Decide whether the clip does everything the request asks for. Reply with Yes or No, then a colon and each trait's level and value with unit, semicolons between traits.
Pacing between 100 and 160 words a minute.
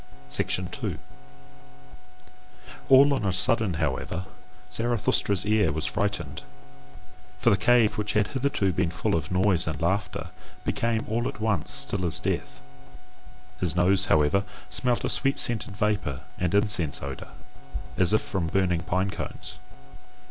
Yes: slow, 135 wpm